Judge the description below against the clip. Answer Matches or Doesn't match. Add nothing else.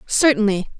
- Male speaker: Doesn't match